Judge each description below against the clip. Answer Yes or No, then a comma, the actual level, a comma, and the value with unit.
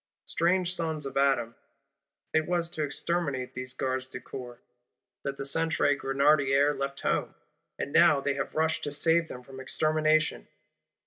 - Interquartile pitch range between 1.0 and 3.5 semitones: Yes, average, 2.9 semitones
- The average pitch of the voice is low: No, medium, 145 Hz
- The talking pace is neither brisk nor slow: Yes, average, 150 wpm